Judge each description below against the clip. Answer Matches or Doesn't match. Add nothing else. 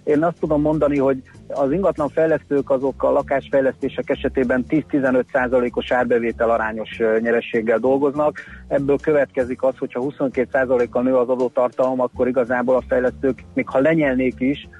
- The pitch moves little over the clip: Matches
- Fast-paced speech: Doesn't match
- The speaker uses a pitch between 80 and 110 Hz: Doesn't match